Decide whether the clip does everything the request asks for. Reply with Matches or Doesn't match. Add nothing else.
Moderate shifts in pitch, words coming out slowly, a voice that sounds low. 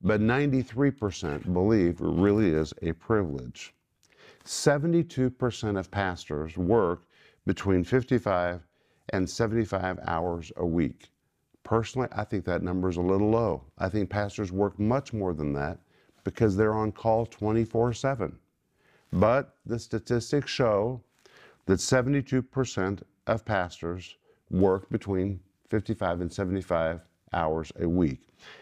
Matches